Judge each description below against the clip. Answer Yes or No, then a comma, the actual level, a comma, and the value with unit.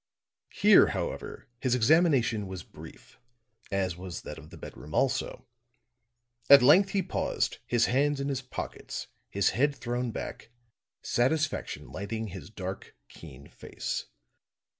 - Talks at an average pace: No, slow, 130 wpm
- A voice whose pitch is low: Yes, low, 120 Hz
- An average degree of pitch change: No, wide, 6.2 semitones